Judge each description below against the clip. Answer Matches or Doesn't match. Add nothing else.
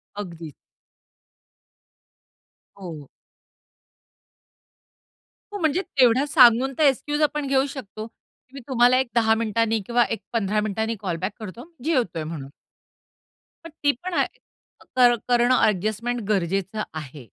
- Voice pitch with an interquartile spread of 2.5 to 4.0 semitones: Doesn't match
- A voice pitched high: Matches